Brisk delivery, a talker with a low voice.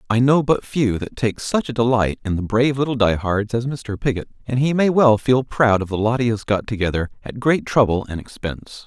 Yes: fast, 245 wpm; low, 115 Hz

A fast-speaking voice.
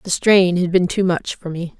Yes: fast, 265 wpm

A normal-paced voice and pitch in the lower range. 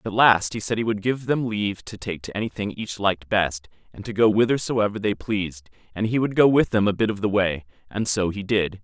No: fast, 250 wpm; low, 105 Hz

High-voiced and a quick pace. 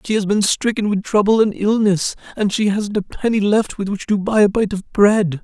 Yes: high, 205 Hz; fast, 245 wpm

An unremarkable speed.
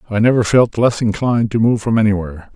No: fast, 210 wpm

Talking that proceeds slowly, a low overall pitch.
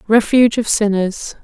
No: slow, 125 wpm; high, 210 Hz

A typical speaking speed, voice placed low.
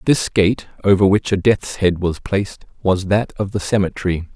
Yes: average, 195 wpm; very low, 95 Hz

